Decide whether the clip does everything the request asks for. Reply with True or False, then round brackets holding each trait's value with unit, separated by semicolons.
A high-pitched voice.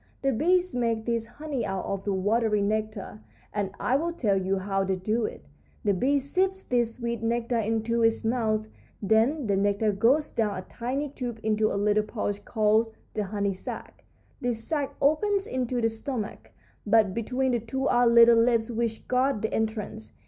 True (225 Hz)